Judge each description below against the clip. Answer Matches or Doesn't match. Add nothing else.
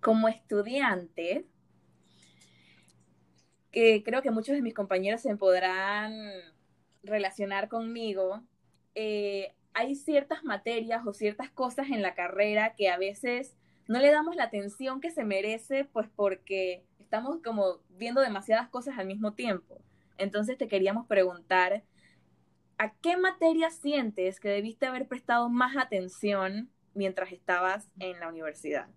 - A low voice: Doesn't match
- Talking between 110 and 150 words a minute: Matches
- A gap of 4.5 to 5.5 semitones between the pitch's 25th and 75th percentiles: Matches